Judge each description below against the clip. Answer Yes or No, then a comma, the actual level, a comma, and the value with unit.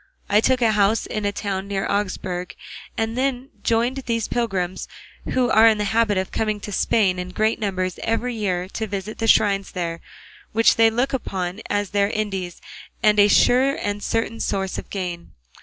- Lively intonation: No, average, 2.9 semitones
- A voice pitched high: Yes, high, 210 Hz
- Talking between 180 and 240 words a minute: Yes, average, 185 wpm